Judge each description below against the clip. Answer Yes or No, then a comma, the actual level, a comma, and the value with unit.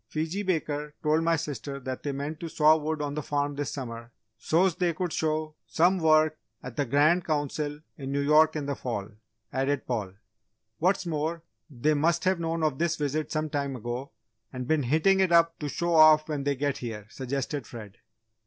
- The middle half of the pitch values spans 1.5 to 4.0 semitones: Yes, narrow, 2.5 semitones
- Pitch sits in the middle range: Yes, medium, 150 Hz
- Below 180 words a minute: No, average, 195 wpm